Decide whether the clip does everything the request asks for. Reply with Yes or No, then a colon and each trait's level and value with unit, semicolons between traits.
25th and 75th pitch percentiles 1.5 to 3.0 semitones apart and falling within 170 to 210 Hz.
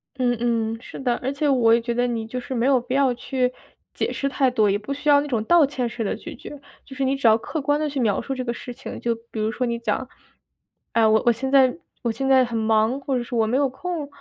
No: average, 2.7 semitones; very high, 250 Hz